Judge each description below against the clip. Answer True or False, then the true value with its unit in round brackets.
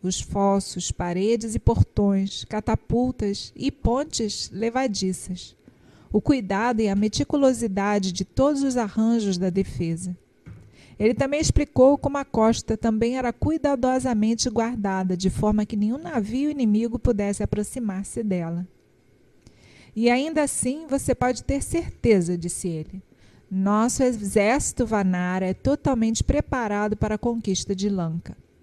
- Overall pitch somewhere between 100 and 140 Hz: False (220 Hz)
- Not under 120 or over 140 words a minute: True (125 wpm)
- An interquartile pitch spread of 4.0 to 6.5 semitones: True (4.5 semitones)